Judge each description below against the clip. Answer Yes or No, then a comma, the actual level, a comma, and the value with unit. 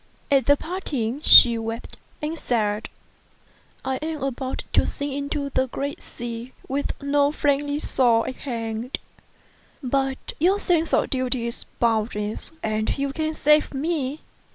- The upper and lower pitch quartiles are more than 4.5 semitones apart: No, average, 3.7 semitones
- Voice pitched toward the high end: Yes, very high, 270 Hz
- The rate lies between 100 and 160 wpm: Yes, average, 140 wpm